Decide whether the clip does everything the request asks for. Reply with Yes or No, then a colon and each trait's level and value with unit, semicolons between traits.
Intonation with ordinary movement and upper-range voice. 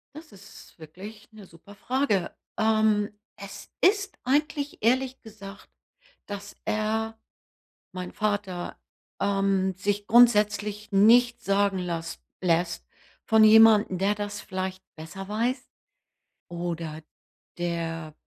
Yes: average, 3.0 semitones; high, 205 Hz